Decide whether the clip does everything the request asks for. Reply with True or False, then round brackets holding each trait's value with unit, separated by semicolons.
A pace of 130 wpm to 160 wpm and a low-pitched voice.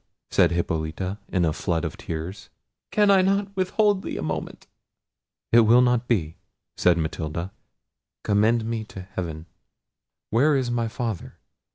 True (140 wpm; 105 Hz)